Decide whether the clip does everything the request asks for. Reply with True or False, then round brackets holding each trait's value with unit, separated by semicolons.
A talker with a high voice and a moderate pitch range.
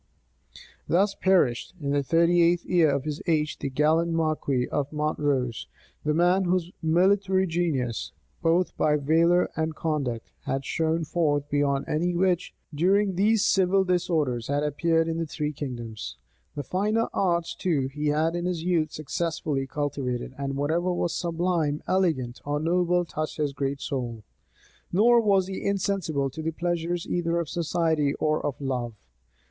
False (160 Hz; 3.5 semitones)